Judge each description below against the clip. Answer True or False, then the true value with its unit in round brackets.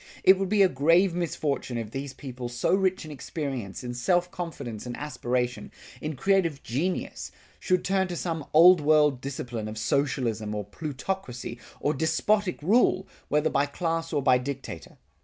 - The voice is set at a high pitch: False (150 Hz)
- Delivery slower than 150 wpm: False (160 wpm)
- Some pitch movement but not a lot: False (6.0 semitones)